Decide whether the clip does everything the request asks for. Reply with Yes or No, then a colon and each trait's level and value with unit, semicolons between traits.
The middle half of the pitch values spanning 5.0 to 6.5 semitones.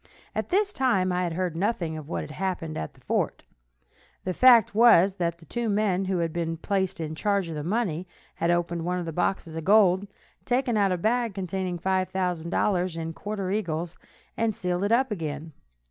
No: average, 3.4 semitones